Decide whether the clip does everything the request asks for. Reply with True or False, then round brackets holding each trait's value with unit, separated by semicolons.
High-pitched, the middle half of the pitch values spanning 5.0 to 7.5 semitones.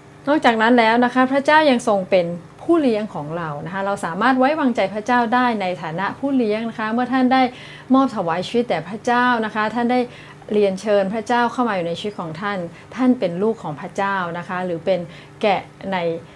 True (215 Hz; 5.4 semitones)